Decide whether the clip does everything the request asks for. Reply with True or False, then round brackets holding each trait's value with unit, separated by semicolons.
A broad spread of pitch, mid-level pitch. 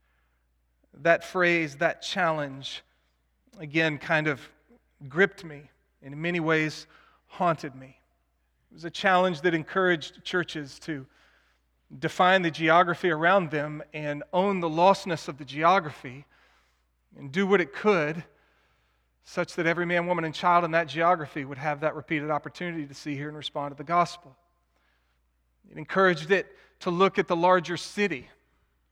False (4.4 semitones; 155 Hz)